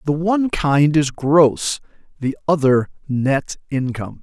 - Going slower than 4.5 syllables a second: Yes, 4.0 syllables/s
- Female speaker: No, male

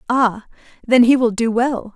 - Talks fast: No, average, 185 wpm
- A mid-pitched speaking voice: No, high, 235 Hz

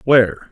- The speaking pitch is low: Yes, low, 120 Hz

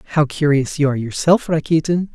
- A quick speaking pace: No, average, 170 wpm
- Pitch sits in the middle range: Yes, medium, 150 Hz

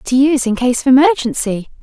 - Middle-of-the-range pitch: No, very high, 255 Hz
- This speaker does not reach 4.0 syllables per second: No, 6.0 syllables/s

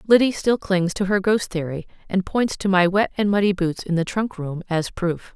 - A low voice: No, high, 190 Hz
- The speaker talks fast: Yes, fast, 235 wpm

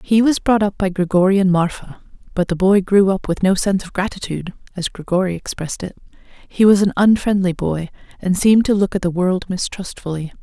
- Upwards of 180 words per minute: Yes, average, 200 wpm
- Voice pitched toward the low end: No, high, 190 Hz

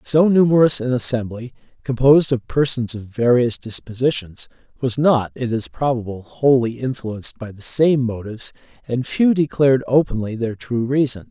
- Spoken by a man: Yes, male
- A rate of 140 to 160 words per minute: Yes, average, 150 wpm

